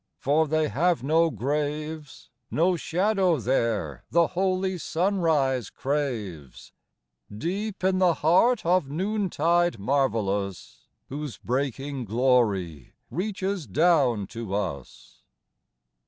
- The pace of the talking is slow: Yes, slow, 95 wpm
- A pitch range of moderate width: No, wide, 6.8 semitones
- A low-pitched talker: No, medium, 150 Hz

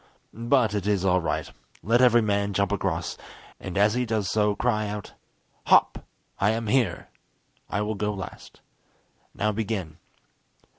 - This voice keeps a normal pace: Yes, average, 150 wpm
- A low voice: Yes, low, 105 Hz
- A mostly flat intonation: Yes, narrow, 1.9 semitones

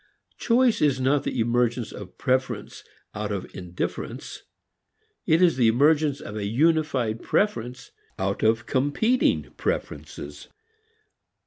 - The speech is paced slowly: Yes, slow, 115 wpm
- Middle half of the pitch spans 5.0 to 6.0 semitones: Yes, wide, 5.4 semitones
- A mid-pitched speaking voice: No, low, 130 Hz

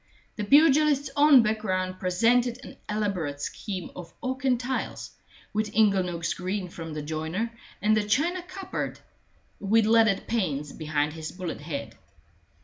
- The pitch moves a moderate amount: No, wide, 6.3 semitones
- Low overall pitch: No, high, 205 Hz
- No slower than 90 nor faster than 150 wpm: Yes, average, 140 wpm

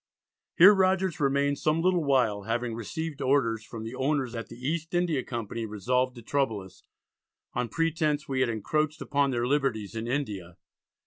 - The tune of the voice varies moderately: Yes, average, 5.0 semitones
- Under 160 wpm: No, average, 170 wpm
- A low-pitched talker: Yes, low, 130 Hz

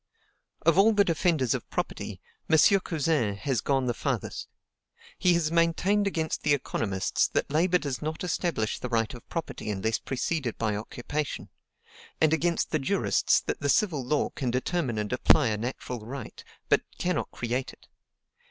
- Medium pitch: Yes, medium, 145 Hz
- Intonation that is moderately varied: No, wide, 5.8 semitones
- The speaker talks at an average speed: Yes, average, 160 wpm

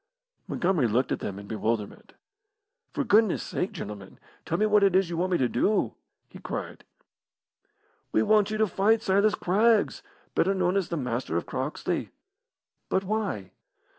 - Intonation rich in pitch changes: Yes, wide, 8.9 semitones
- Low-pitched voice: No, medium, 185 Hz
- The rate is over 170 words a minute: No, average, 165 wpm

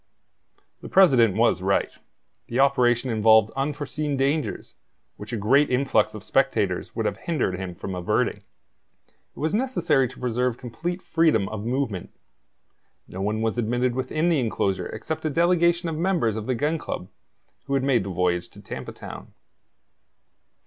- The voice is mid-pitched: No, low, 125 Hz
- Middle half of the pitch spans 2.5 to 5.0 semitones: No, wide, 5.6 semitones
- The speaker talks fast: No, average, 155 wpm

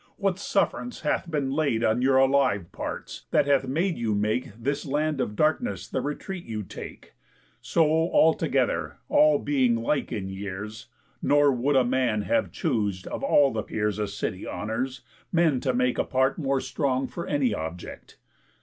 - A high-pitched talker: No, low, 135 Hz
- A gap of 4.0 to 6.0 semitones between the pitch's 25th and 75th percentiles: Yes, average, 5.1 semitones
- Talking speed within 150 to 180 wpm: Yes, average, 170 wpm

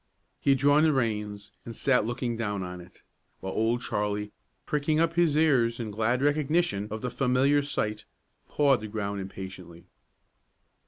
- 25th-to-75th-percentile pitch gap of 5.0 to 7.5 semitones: Yes, wide, 5.5 semitones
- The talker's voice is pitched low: Yes, low, 115 Hz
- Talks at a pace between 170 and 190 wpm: No, average, 160 wpm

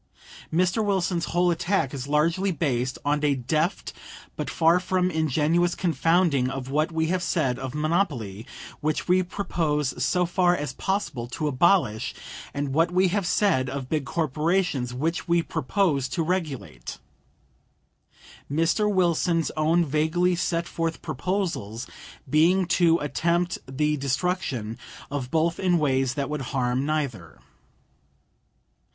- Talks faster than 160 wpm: No, slow, 135 wpm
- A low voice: No, medium, 160 Hz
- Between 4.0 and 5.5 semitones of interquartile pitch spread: Yes, average, 4.6 semitones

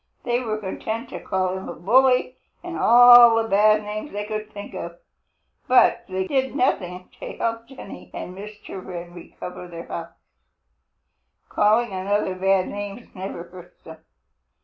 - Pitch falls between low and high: No, high, 205 Hz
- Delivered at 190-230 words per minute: No, average, 150 wpm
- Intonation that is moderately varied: Yes, average, 3.8 semitones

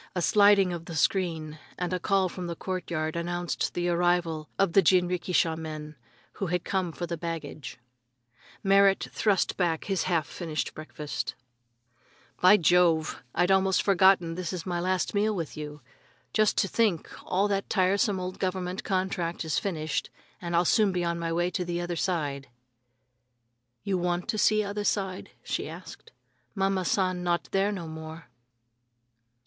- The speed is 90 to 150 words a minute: No, average, 165 wpm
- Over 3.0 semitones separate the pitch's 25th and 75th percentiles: No, narrow, 2.4 semitones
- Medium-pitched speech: Yes, medium, 180 Hz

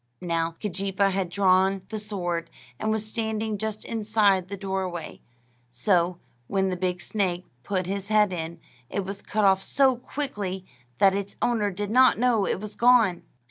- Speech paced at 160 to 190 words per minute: Yes, average, 165 wpm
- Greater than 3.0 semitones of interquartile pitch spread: No, narrow, 2.6 semitones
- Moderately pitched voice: No, high, 195 Hz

